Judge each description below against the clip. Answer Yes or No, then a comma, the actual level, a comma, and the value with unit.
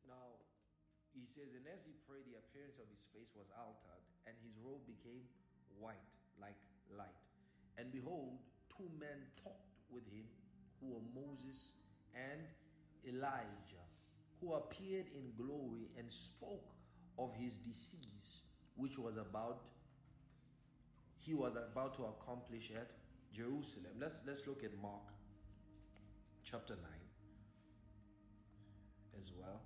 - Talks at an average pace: No, slow, 125 wpm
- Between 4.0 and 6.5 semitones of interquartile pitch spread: Yes, average, 4.4 semitones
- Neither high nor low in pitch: No, low, 115 Hz